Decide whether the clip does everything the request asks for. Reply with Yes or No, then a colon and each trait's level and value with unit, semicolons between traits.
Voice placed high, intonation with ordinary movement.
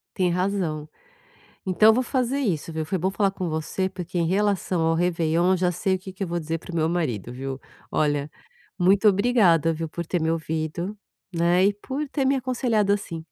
No: medium, 180 Hz; average, 3.6 semitones